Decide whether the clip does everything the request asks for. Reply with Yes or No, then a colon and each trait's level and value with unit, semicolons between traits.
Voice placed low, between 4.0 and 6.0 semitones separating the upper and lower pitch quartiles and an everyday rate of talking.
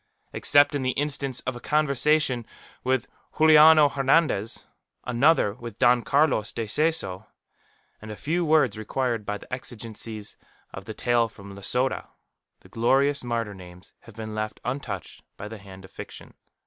Yes: low, 120 Hz; average, 4.9 semitones; average, 150 wpm